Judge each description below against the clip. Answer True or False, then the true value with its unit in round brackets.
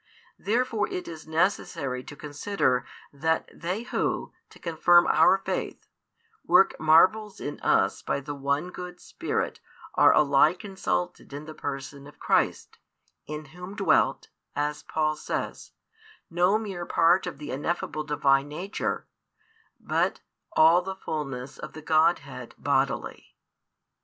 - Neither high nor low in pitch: True (155 Hz)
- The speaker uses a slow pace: True (130 wpm)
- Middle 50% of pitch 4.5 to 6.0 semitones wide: False (3.8 semitones)